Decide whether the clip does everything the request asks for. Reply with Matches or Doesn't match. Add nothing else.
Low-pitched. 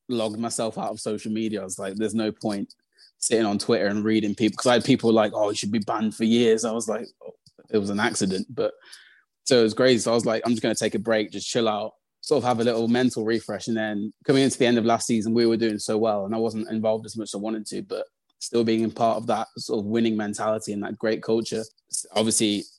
Matches